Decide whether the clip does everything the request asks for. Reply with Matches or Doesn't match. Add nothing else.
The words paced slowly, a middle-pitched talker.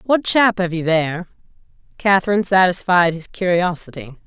Matches